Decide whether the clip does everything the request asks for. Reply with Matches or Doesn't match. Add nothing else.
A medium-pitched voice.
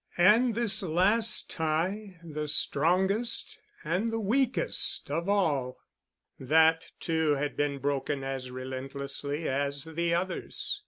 Matches